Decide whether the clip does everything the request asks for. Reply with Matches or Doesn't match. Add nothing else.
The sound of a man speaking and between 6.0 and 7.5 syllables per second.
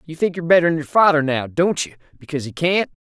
Matches